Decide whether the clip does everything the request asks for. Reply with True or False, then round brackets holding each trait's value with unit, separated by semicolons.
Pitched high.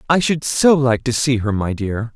False (125 Hz)